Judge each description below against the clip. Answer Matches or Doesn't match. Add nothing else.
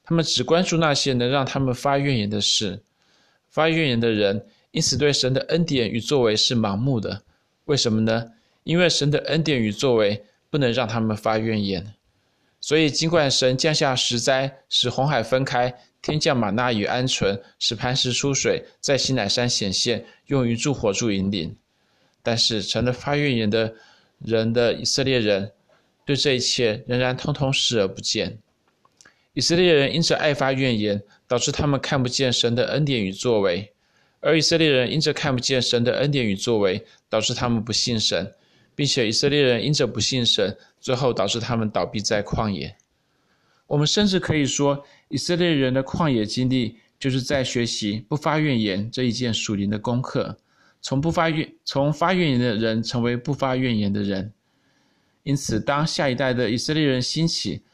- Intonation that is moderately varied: Matches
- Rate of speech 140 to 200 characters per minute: Doesn't match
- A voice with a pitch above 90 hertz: Matches